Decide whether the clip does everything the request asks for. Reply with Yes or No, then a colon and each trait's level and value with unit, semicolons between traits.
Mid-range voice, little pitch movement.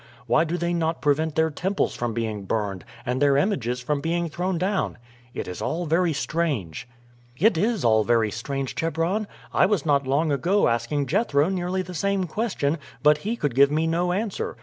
No: medium, 160 Hz; average, 5.0 semitones